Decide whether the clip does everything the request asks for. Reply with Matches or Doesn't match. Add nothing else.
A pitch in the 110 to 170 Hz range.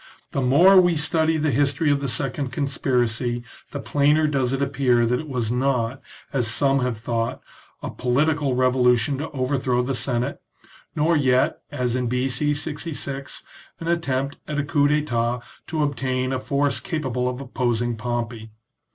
Matches